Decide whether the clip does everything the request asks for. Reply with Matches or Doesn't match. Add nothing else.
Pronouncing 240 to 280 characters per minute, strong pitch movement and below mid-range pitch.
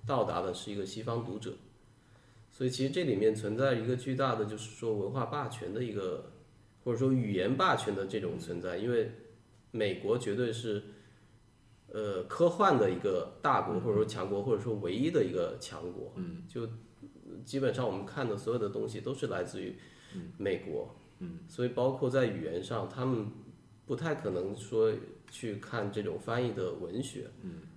Matches